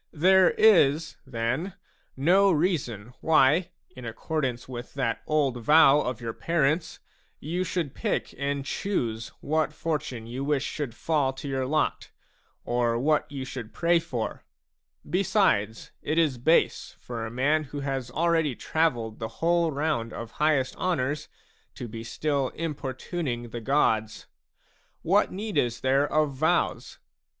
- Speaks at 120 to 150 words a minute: Yes, average, 140 wpm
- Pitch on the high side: No, medium, 140 Hz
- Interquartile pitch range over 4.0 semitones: Yes, average, 4.7 semitones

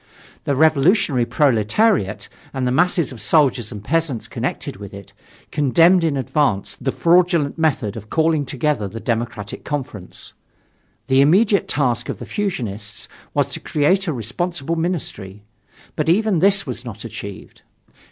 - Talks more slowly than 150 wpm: Yes, average, 140 wpm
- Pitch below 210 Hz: Yes, medium, 140 Hz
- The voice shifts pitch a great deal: Yes, wide, 6.6 semitones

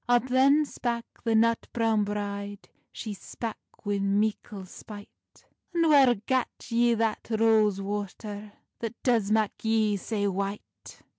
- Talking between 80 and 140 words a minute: Yes, slow, 135 wpm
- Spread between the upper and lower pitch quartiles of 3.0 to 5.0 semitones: No, narrow, 2.4 semitones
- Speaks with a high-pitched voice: Yes, high, 220 Hz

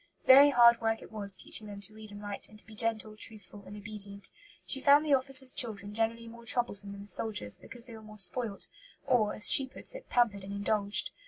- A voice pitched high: Yes, high, 215 Hz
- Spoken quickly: Yes, fast, 225 wpm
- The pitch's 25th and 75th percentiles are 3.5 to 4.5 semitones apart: No, average, 2.7 semitones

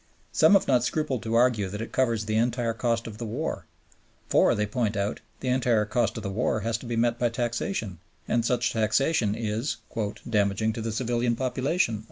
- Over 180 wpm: Yes, average, 200 wpm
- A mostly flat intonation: Yes, narrow, 2.3 semitones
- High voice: No, low, 115 Hz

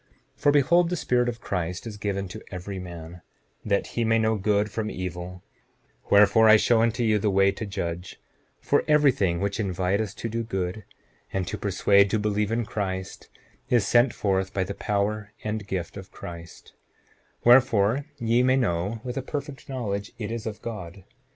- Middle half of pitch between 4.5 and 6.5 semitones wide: No, average, 3.4 semitones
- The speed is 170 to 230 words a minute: Yes, average, 185 wpm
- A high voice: No, low, 105 Hz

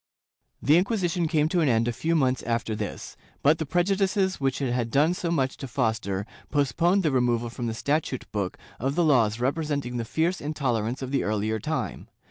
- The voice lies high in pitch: No, low, 135 Hz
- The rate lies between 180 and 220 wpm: Yes, average, 200 wpm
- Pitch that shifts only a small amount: No, wide, 5.6 semitones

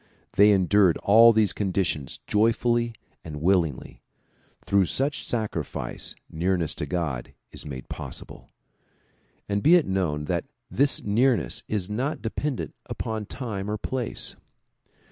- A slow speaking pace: Yes, slow, 125 wpm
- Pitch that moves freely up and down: No, average, 4.9 semitones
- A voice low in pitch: Yes, low, 100 Hz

